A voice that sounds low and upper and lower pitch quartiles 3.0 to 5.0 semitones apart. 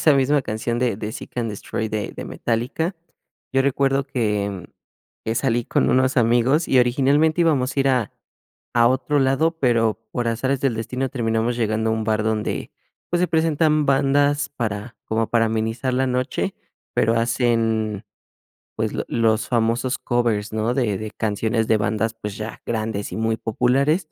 Yes: low, 120 Hz; average, 3.4 semitones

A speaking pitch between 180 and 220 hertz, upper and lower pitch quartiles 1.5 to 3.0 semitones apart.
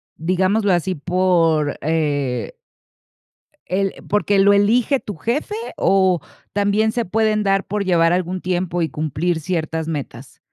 No: medium, 185 Hz; average, 3.9 semitones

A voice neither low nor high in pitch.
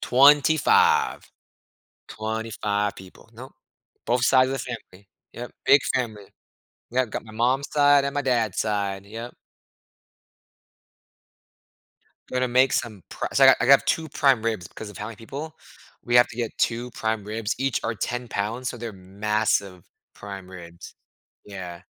No: low, 115 Hz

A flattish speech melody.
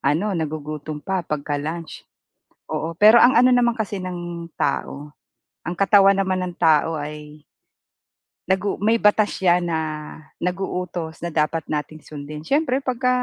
No: average, 4.7 semitones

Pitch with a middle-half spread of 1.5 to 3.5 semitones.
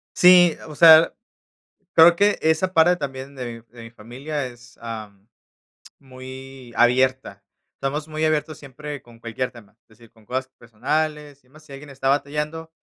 No: average, 4.3 semitones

